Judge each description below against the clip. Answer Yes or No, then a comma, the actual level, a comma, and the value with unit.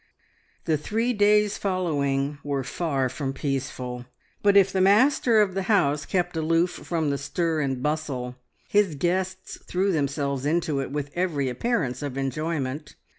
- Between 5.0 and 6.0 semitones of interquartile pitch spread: Yes, average, 5.3 semitones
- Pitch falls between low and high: Yes, medium, 155 Hz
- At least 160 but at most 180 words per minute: No, average, 150 wpm